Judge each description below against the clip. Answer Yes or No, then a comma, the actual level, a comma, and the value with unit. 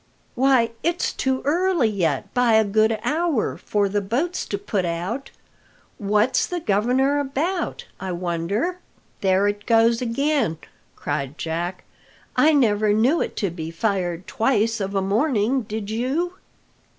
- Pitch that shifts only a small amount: No, wide, 5.6 semitones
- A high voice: Yes, high, 220 Hz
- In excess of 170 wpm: No, average, 140 wpm